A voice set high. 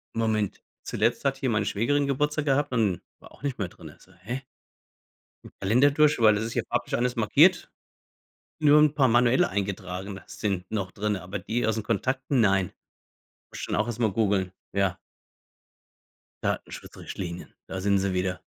No: low, 110 Hz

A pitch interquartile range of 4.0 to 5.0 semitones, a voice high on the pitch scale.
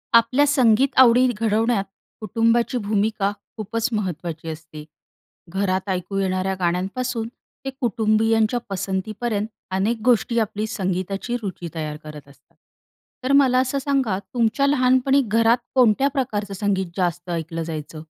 Yes: average, 4.3 semitones; high, 215 Hz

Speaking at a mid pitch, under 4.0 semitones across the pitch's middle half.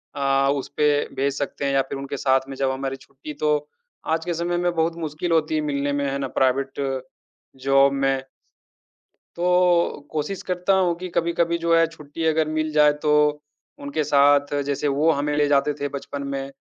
Yes: medium, 145 Hz; average, 2.7 semitones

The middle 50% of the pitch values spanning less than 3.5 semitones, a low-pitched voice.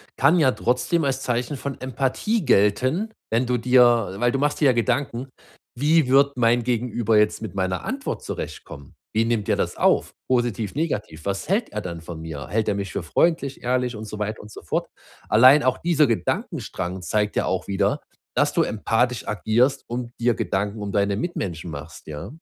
No: average, 4.4 semitones; low, 120 Hz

